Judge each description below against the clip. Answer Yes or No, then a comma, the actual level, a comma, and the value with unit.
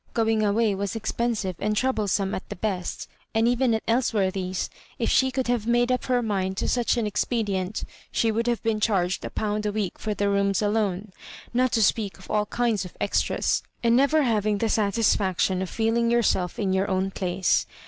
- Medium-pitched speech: No, high, 215 Hz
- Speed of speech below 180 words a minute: No, average, 200 wpm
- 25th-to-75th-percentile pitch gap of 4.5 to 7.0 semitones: No, average, 3.2 semitones